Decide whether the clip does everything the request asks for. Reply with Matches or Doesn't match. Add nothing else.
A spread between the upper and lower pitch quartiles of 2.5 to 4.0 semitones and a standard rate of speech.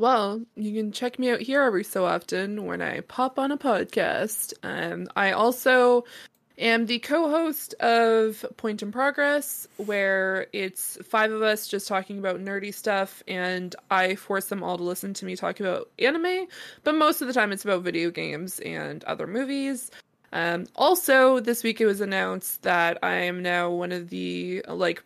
Doesn't match